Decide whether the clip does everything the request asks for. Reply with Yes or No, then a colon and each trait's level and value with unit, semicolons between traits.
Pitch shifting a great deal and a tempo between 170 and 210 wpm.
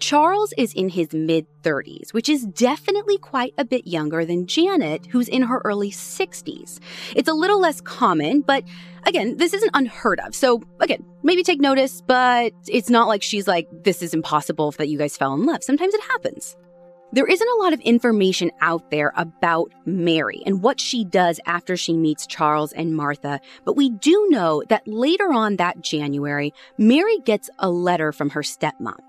Yes: wide, 8.6 semitones; average, 185 wpm